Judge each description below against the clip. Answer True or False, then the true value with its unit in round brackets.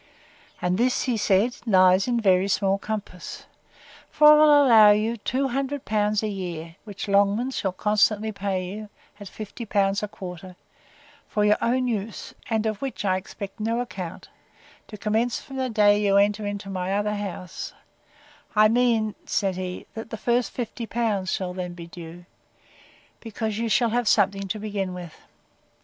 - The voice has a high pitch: True (210 Hz)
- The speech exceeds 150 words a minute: True (170 wpm)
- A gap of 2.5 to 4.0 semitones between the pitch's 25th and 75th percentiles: True (2.9 semitones)